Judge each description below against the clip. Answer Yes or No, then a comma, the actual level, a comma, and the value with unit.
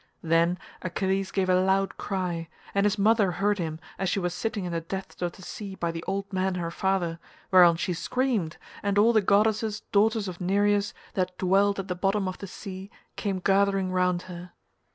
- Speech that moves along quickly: No, average, 195 wpm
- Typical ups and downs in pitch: No, narrow, 2.0 semitones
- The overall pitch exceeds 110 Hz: Yes, high, 190 Hz